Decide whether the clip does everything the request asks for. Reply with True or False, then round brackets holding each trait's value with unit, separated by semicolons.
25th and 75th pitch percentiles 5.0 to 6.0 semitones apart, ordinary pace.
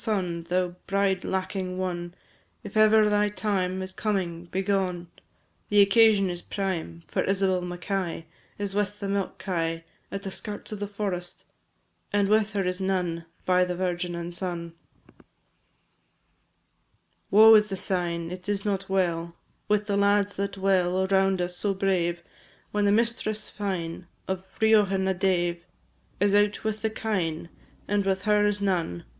False (2.4 semitones; 155 wpm)